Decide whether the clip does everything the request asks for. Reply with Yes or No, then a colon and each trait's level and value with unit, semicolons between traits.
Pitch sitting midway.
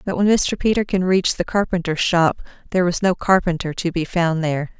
Yes: medium, 175 Hz